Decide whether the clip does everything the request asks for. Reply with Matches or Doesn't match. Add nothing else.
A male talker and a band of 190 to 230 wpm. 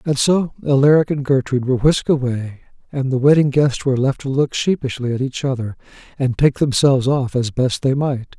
Matches